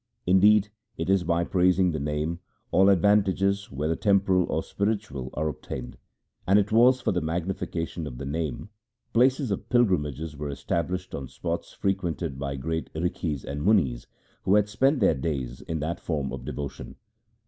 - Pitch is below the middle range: Yes, very low, 85 Hz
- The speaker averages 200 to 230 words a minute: No, average, 160 wpm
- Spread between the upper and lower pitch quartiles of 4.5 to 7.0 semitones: Yes, average, 4.8 semitones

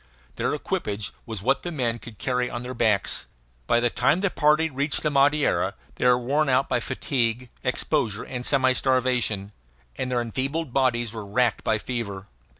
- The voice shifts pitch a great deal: No, average, 2.9 semitones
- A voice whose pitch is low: Yes, low, 125 Hz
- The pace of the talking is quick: No, average, 175 wpm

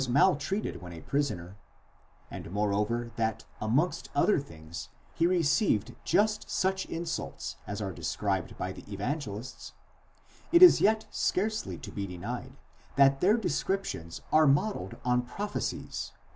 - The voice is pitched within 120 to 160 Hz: Yes, medium, 140 Hz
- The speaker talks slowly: Yes, slow, 130 wpm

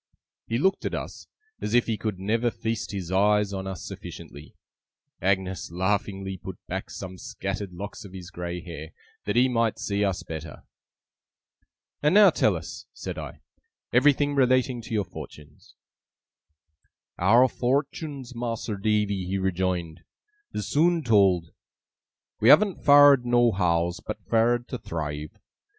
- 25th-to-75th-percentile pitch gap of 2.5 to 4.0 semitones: No, average, 4.7 semitones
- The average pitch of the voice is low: Yes, low, 105 Hz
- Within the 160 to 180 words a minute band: No, average, 140 wpm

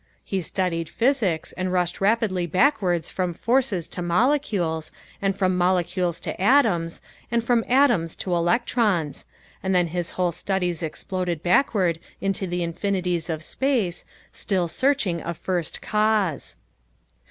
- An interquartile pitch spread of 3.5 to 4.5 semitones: Yes, average, 3.8 semitones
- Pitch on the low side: No, medium, 185 Hz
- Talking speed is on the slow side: Yes, slow, 130 wpm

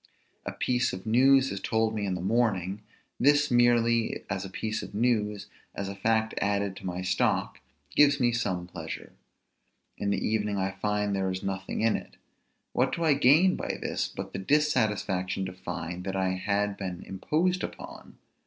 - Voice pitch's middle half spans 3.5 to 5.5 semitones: Yes, average, 4.1 semitones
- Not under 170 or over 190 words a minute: Yes, average, 180 wpm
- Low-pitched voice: Yes, low, 105 Hz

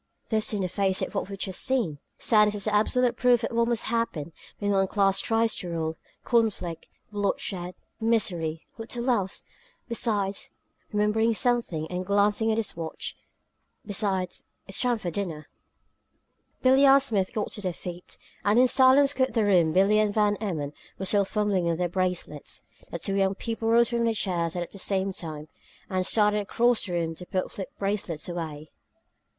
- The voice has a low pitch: No, high, 200 Hz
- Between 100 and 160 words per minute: No, average, 175 wpm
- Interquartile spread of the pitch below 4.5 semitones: Yes, average, 3.9 semitones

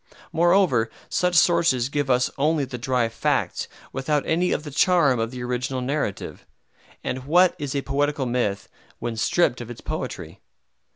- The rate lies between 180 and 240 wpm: No, average, 160 wpm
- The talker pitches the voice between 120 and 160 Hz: Yes, low, 135 Hz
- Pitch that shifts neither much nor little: Yes, average, 4.2 semitones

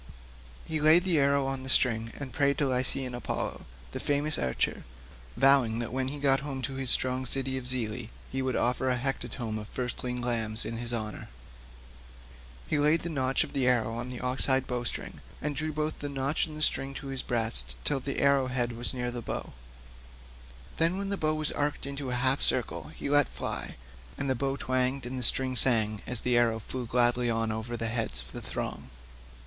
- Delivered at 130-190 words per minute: No, fast, 205 wpm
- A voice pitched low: Yes, low, 130 Hz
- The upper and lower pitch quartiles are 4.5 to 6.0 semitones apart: No, narrow, 2.6 semitones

